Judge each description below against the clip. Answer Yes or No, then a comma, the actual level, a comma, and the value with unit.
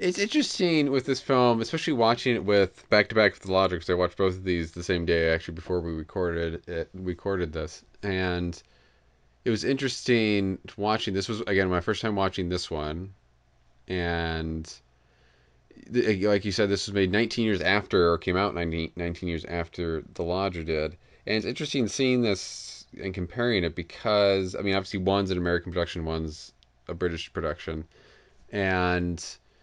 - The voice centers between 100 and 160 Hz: No, very low, 90 Hz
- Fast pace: No, average, 180 wpm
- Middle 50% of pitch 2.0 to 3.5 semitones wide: No, average, 4.0 semitones